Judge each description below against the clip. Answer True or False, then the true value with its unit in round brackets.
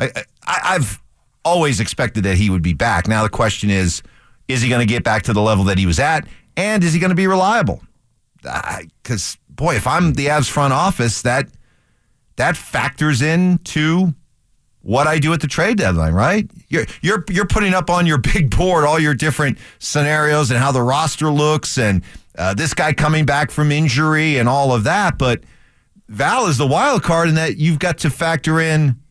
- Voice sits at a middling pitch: True (150 Hz)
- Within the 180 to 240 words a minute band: True (200 wpm)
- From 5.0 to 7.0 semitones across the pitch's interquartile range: True (5.4 semitones)